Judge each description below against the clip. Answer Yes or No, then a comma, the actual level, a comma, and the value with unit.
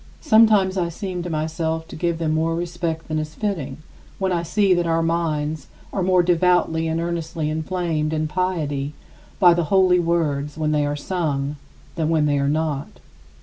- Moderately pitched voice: Yes, medium, 165 Hz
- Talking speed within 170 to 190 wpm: Yes, average, 180 wpm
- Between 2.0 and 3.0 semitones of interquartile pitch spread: Yes, narrow, 2.4 semitones